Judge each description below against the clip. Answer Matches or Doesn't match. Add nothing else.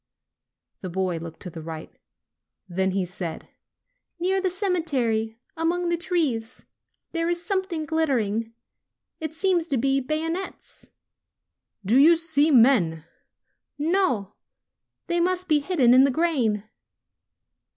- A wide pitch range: Matches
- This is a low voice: Doesn't match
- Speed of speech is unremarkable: Doesn't match